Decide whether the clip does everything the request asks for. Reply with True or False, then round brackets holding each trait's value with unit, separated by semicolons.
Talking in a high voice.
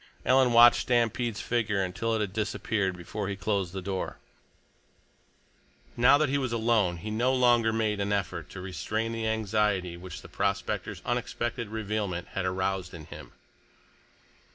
False (105 Hz)